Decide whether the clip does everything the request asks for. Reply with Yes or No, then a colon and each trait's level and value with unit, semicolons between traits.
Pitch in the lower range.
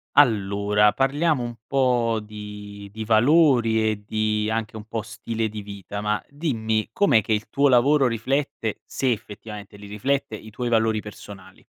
Yes: low, 110 Hz